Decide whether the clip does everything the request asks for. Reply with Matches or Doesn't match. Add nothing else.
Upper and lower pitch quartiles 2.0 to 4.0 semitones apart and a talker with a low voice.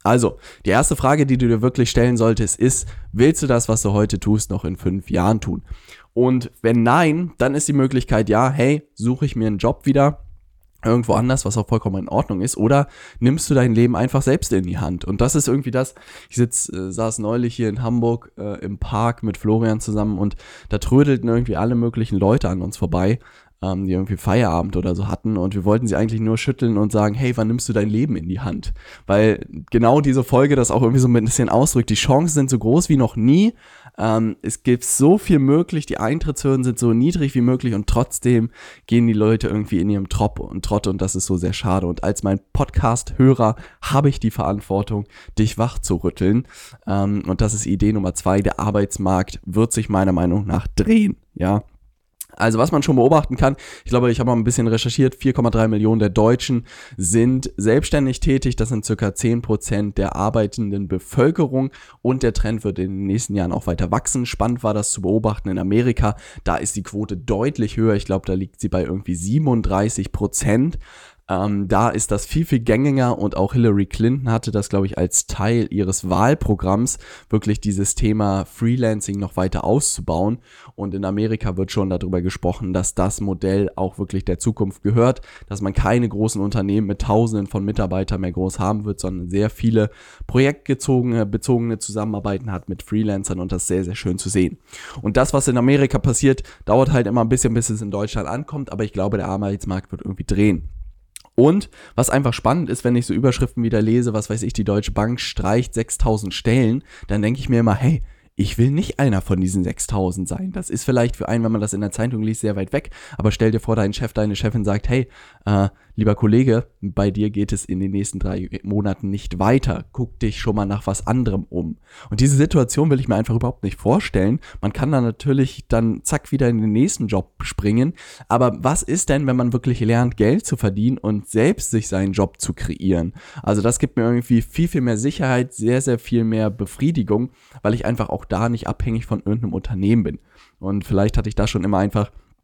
Matches